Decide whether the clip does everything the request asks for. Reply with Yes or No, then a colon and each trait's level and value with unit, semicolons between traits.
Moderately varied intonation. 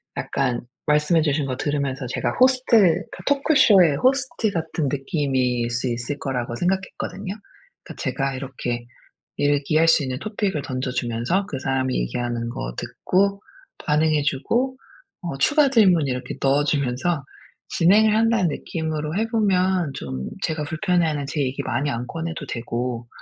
No: wide, 6.2 semitones